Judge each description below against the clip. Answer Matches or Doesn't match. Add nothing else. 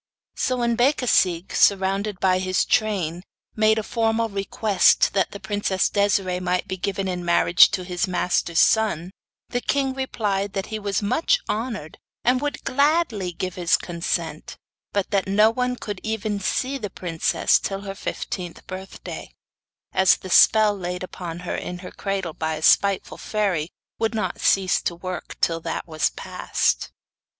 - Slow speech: Doesn't match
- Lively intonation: Doesn't match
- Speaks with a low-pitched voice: Doesn't match